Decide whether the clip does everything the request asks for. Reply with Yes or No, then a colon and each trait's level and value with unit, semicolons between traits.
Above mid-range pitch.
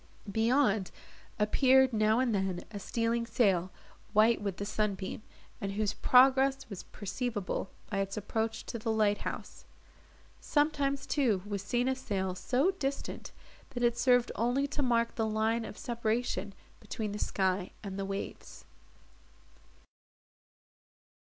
Yes: high, 220 Hz